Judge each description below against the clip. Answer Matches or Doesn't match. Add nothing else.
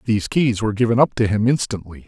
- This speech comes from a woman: Doesn't match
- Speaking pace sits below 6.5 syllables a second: Doesn't match